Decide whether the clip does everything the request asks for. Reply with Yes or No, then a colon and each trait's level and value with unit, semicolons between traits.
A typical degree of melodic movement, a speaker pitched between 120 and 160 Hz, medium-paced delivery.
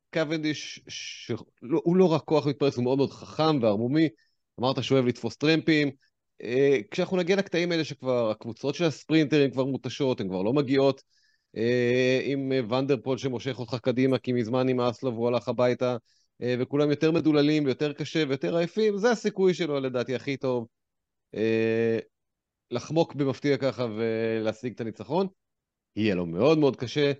No: average, 3.9 semitones; low, 135 Hz; fast, 160 wpm